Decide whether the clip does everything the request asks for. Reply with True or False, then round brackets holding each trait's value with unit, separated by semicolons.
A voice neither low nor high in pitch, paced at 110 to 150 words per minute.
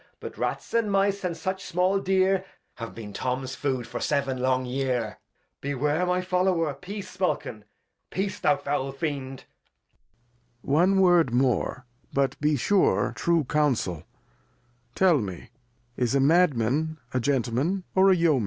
True (150 Hz; 145 wpm)